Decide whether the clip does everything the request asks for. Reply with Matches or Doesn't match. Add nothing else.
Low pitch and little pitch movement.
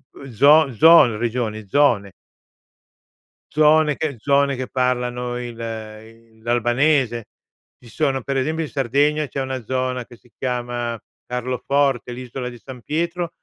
Doesn't match